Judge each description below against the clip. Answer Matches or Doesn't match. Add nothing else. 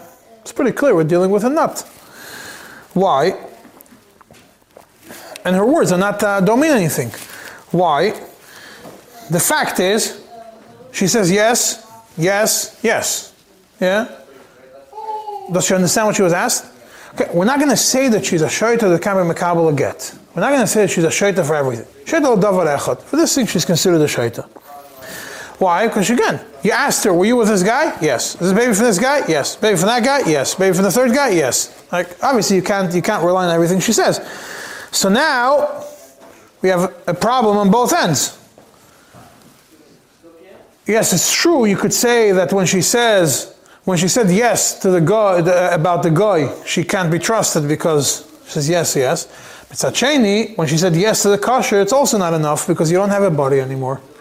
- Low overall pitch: Doesn't match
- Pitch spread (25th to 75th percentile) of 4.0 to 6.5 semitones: Matches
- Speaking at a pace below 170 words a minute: Doesn't match